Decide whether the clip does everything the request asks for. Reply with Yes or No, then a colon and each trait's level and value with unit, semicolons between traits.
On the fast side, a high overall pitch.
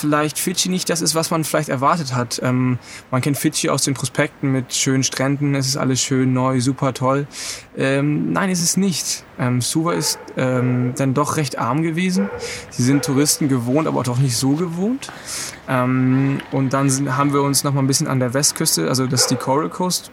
No: fast, 210 wpm; medium, 140 Hz